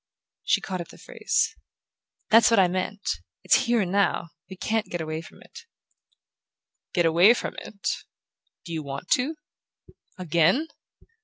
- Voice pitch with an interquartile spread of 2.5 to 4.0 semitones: No, average, 4.9 semitones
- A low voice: No, medium, 185 Hz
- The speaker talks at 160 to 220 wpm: No, average, 150 wpm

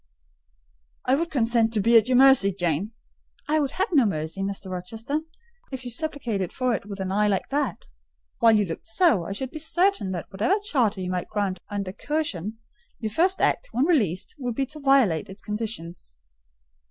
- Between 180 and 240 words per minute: Yes, average, 190 wpm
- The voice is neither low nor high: No, high, 225 Hz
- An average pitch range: No, wide, 6.0 semitones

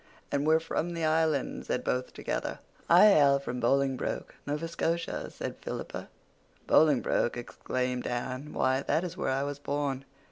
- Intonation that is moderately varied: Yes, average, 3.5 semitones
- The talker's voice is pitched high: No, medium, 140 Hz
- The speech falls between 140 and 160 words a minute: Yes, average, 150 wpm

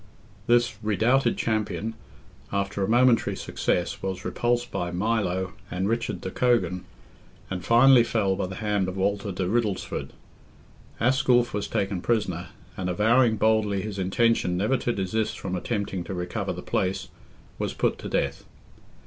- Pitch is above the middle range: No, low, 105 Hz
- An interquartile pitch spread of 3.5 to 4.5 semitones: Yes, average, 3.8 semitones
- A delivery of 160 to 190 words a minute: No, average, 150 wpm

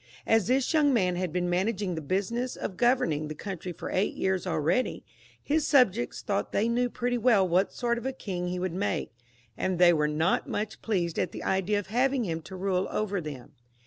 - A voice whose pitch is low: No, high, 190 Hz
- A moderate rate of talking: No, fast, 210 wpm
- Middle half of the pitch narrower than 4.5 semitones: No, average, 5.0 semitones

